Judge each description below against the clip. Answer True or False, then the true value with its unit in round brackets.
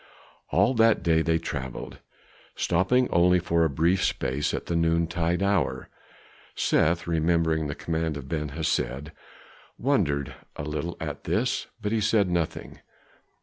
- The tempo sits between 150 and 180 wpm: False (140 wpm)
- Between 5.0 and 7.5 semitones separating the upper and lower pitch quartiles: False (2.8 semitones)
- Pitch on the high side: False (85 Hz)